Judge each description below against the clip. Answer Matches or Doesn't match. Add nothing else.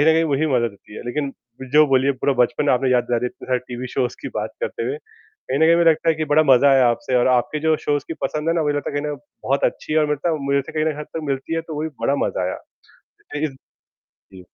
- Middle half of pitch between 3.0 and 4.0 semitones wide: Matches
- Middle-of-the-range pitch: Matches